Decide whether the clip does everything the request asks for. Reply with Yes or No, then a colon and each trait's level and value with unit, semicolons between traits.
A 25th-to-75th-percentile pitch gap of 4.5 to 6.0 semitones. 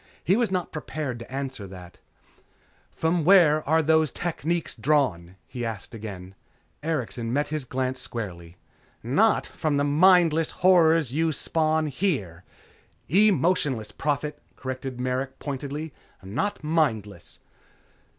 Yes: average, 5.3 semitones